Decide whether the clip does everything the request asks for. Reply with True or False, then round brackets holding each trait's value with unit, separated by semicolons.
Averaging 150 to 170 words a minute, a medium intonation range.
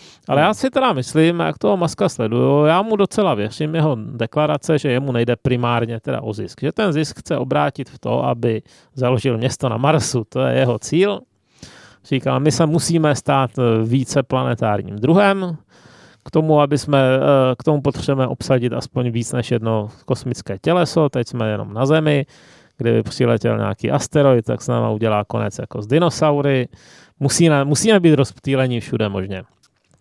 True (165 wpm; 4.5 semitones)